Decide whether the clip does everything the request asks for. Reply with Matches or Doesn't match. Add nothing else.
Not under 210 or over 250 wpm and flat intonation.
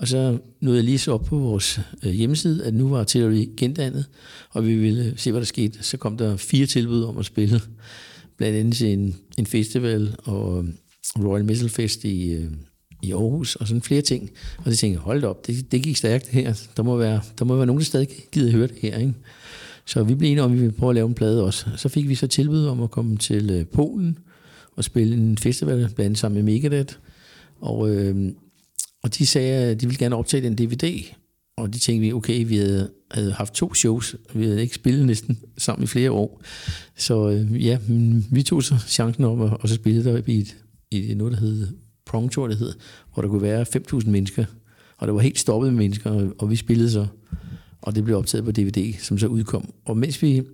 Doesn't match